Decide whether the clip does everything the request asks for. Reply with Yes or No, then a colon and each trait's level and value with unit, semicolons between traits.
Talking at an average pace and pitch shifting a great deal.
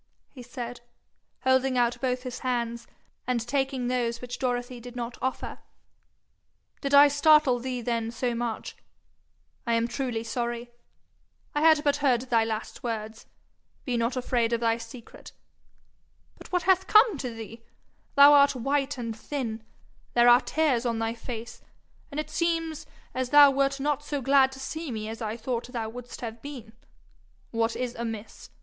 No: average, 160 wpm; average, 2.9 semitones